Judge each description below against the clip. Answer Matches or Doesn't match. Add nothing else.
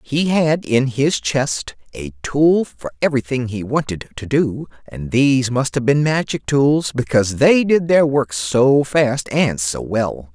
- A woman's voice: Doesn't match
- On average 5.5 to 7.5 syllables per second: Doesn't match